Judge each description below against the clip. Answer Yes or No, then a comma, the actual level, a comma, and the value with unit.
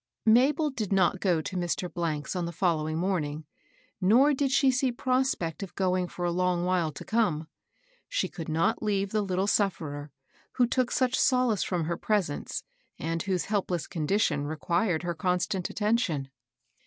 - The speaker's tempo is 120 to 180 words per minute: Yes, average, 175 wpm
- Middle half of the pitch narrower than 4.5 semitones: No, average, 4.9 semitones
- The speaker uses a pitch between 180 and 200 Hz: Yes, medium, 185 Hz